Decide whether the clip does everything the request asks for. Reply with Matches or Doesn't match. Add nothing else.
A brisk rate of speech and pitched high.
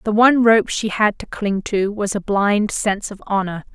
Matches